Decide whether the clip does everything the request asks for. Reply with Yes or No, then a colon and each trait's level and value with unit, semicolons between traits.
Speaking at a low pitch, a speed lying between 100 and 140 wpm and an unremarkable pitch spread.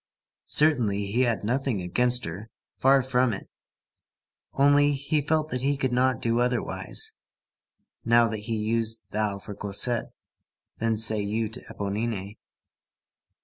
Yes: low, 115 Hz; slow, 135 wpm; average, 3.5 semitones